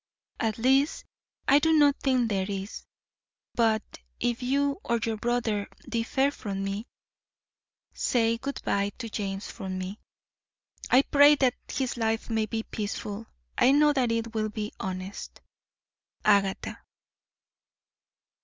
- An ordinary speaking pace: No, slow, 130 wpm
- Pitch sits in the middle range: No, high, 225 Hz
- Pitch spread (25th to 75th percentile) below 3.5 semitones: No, average, 4.2 semitones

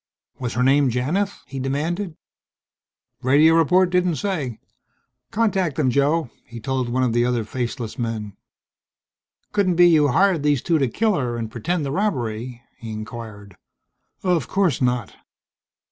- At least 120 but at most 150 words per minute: Yes, average, 145 wpm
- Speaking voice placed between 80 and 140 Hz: Yes, low, 135 Hz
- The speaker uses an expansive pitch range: Yes, wide, 6.5 semitones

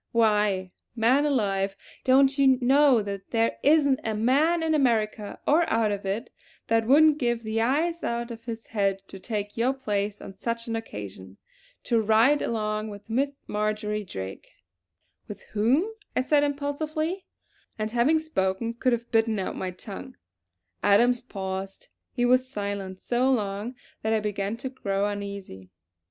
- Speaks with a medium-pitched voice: No, high, 225 Hz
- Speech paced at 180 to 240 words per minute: No, average, 155 wpm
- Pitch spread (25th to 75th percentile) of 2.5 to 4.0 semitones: No, average, 4.5 semitones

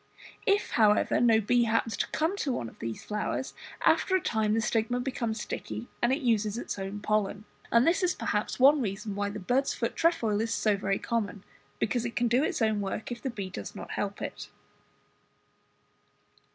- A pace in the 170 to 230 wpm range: Yes, average, 195 wpm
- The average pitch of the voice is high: Yes, high, 225 Hz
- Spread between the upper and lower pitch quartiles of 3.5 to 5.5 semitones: No, average, 3.0 semitones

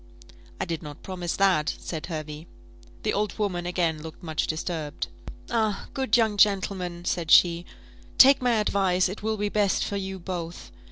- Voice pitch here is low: No, medium, 185 Hz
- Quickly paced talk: No, average, 165 wpm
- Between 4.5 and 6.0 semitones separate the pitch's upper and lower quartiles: No, average, 3.6 semitones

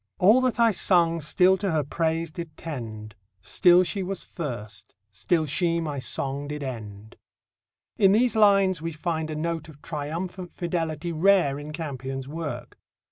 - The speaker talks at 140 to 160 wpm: Yes, average, 155 wpm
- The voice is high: No, medium, 165 Hz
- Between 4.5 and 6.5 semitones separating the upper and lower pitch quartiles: No, average, 3.9 semitones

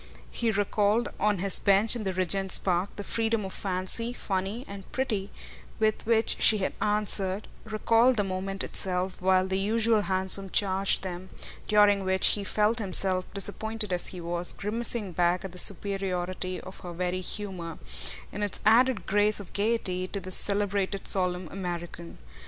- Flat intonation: Yes, narrow, 2.3 semitones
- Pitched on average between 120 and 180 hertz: No, high, 195 Hz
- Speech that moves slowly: No, average, 160 wpm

